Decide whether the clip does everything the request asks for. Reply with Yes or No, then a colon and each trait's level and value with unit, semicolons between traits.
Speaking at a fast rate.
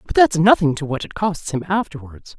Yes: fast, 225 wpm